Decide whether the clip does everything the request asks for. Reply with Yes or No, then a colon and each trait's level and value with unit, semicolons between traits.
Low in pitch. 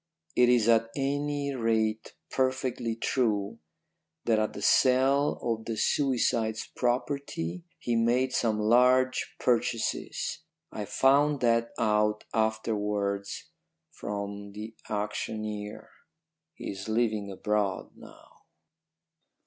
Yes: low, 115 Hz